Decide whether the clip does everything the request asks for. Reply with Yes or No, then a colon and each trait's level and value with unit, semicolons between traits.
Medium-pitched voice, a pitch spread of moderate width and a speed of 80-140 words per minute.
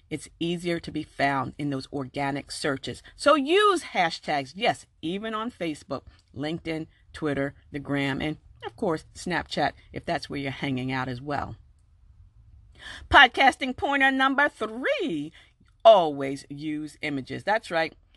No: medium, 150 Hz; wide, 8.1 semitones; slow, 135 wpm